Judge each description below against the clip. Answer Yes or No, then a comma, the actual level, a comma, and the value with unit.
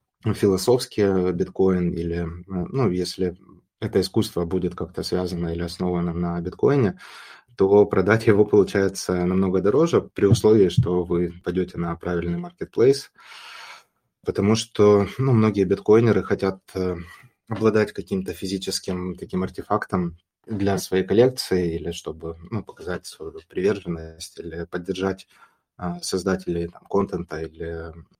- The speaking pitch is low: Yes, very low, 95 Hz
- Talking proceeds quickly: No, average, 115 wpm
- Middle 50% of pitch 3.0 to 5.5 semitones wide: No, narrow, 2.5 semitones